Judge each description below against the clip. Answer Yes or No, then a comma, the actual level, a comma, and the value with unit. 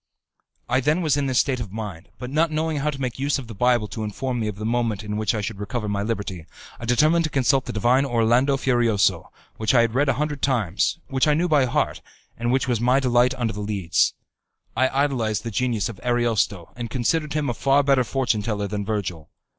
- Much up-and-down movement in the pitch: No, average, 4.1 semitones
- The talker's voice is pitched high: No, low, 120 Hz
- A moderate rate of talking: No, fast, 230 wpm